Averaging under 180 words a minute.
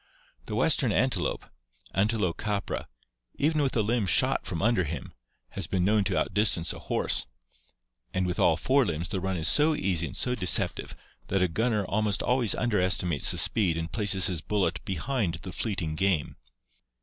Yes: average, 170 wpm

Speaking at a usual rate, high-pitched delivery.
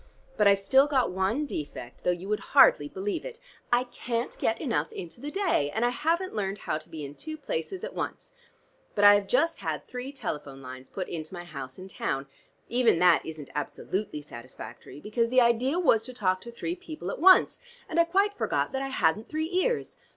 No: fast, 210 wpm; high, 220 Hz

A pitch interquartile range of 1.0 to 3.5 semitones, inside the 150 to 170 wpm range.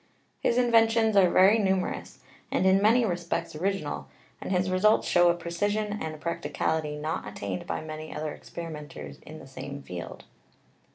No: average, 4.6 semitones; average, 155 wpm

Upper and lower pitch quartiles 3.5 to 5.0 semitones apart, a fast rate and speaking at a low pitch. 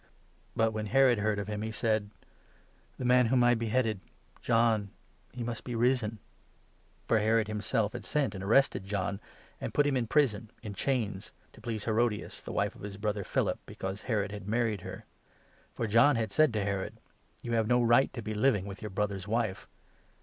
No: narrow, 2.6 semitones; fast, 210 wpm; low, 110 Hz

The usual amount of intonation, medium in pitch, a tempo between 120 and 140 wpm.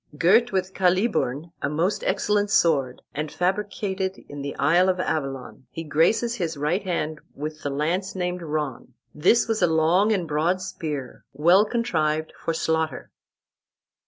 No: average, 3.9 semitones; medium, 170 Hz; average, 150 wpm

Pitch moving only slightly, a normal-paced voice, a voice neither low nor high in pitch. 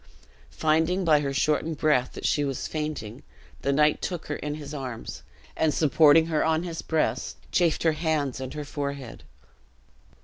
Yes: narrow, 2.2 semitones; average, 165 wpm; medium, 150 Hz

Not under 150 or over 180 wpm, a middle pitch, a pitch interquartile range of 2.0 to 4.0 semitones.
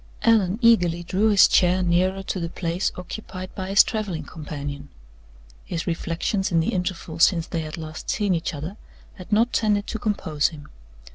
Yes: average, 170 wpm; medium, 180 Hz; average, 3.5 semitones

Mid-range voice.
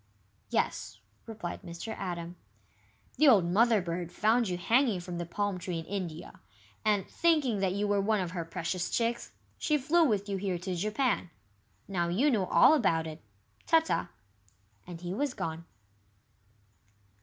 No: high, 195 Hz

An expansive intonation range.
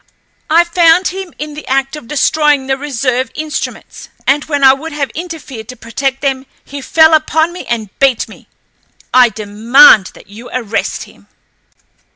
No: average, 3.7 semitones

